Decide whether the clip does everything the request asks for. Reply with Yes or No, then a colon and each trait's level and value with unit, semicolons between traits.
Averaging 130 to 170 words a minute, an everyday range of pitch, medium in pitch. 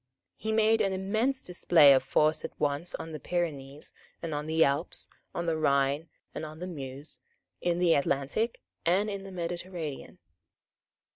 Yes: average, 160 wpm; average, 4.3 semitones; medium, 165 Hz